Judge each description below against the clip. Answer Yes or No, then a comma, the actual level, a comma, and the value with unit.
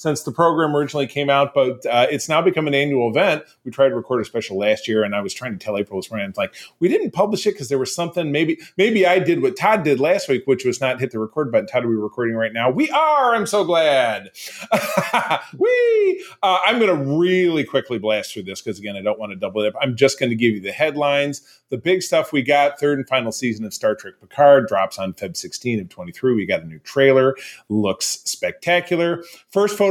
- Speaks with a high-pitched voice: No, medium, 140 Hz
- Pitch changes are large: Yes, wide, 7.5 semitones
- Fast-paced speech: Yes, fast, 250 wpm